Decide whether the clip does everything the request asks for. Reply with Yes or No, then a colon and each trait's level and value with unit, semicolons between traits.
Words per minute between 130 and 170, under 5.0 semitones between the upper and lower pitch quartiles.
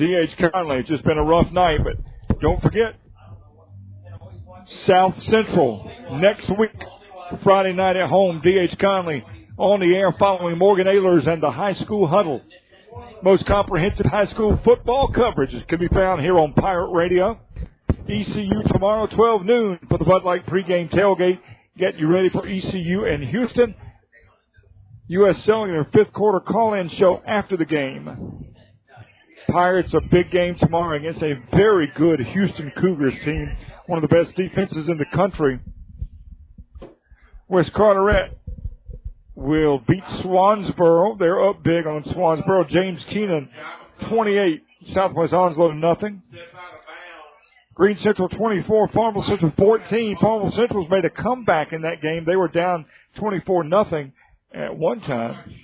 Yes: average, 140 wpm; average, 4.1 semitones